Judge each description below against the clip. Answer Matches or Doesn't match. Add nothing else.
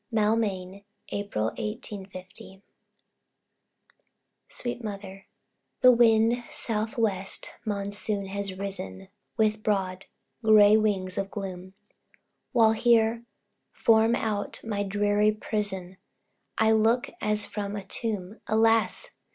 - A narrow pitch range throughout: Matches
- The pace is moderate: Doesn't match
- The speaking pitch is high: Matches